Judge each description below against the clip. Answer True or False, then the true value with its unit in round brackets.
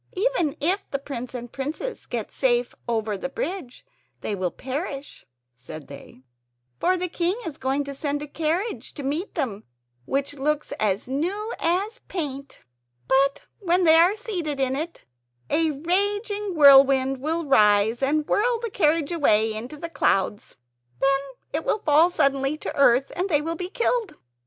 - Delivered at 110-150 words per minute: False (160 wpm)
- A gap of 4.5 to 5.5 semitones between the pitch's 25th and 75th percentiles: True (4.9 semitones)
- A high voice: True (290 Hz)